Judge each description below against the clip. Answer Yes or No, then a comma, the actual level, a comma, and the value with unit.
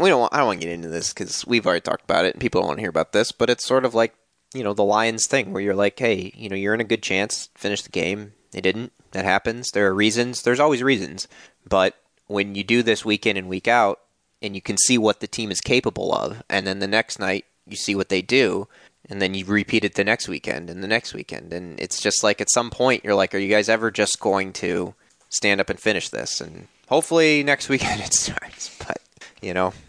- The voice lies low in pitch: Yes, low, 105 Hz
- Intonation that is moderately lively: Yes, average, 3.5 semitones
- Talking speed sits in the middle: No, fast, 260 wpm